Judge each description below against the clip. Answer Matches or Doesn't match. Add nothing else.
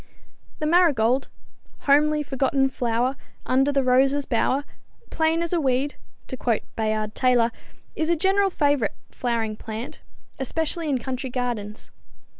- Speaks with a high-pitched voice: Matches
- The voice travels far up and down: Doesn't match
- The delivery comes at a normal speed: Doesn't match